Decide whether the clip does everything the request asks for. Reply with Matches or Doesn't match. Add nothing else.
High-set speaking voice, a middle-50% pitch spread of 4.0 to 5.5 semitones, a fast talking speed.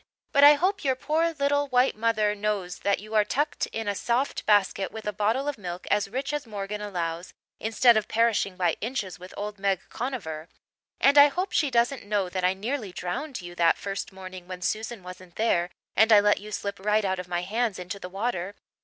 Matches